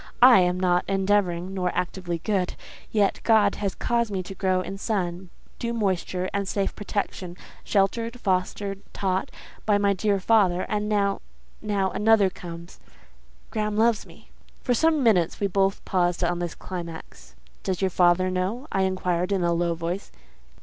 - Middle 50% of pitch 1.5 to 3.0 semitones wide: Yes, narrow, 2.5 semitones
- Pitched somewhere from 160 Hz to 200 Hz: Yes, high, 190 Hz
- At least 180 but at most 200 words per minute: No, average, 155 wpm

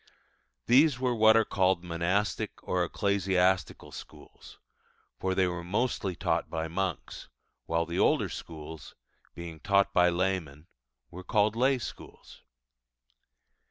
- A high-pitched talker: No, very low, 95 Hz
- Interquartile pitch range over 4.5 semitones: No, average, 3.4 semitones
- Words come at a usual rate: No, slow, 125 wpm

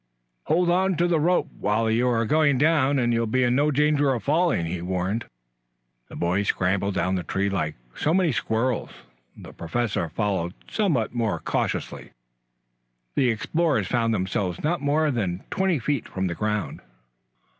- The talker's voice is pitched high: No, low, 120 Hz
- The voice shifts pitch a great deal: Yes, wide, 7.3 semitones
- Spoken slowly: No, average, 165 wpm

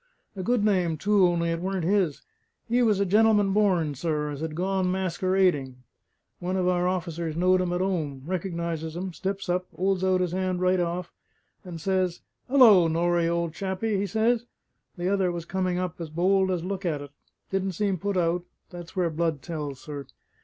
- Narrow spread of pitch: Yes, narrow, 2.3 semitones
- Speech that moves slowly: No, average, 190 wpm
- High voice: No, medium, 180 Hz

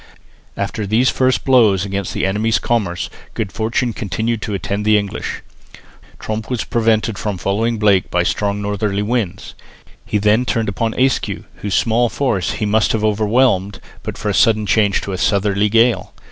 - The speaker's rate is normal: Yes, average, 170 wpm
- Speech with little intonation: Yes, narrow, 2.2 semitones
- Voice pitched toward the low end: Yes, low, 105 Hz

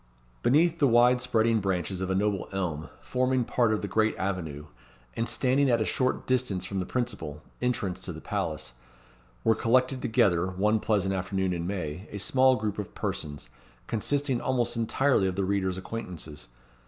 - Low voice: Yes, low, 105 Hz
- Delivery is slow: No, average, 170 wpm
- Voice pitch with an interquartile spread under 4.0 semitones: No, average, 4.9 semitones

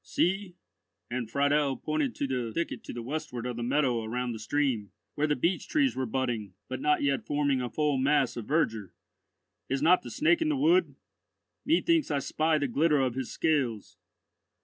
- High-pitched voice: No, medium, 140 Hz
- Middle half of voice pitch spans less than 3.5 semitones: No, average, 4.2 semitones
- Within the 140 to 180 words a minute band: No, average, 190 wpm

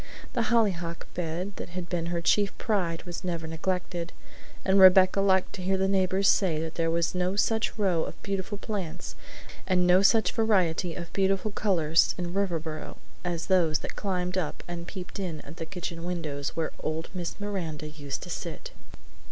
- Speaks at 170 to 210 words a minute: Yes, average, 175 wpm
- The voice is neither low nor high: Yes, medium, 180 Hz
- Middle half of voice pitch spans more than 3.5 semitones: No, average, 2.7 semitones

